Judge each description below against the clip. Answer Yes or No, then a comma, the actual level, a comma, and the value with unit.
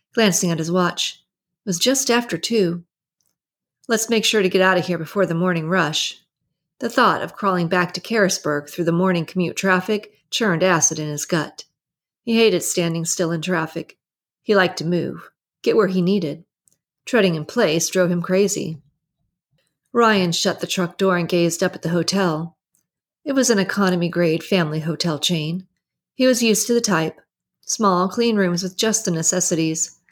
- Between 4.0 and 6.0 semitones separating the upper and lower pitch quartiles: No, average, 2.9 semitones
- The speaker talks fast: No, average, 180 wpm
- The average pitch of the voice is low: No, medium, 180 Hz